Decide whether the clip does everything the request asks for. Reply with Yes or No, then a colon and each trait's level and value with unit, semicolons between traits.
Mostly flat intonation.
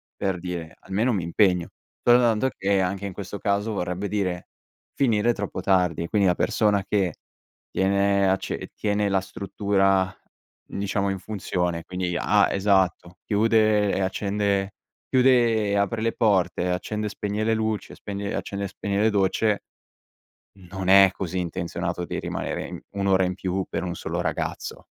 Yes: narrow, 2.0 semitones